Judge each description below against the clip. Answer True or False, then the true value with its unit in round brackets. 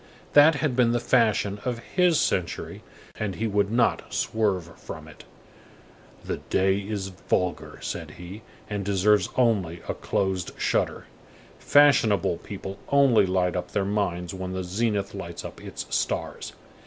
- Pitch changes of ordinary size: True (3.7 semitones)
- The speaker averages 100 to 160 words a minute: True (145 wpm)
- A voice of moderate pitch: False (100 Hz)